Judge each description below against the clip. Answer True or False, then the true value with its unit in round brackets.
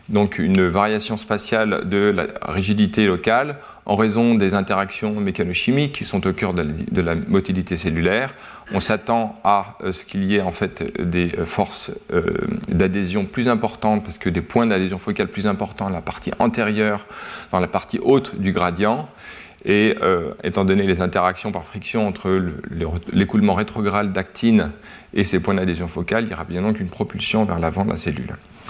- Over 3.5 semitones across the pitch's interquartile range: False (2.4 semitones)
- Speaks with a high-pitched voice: False (100 Hz)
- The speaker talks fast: False (175 wpm)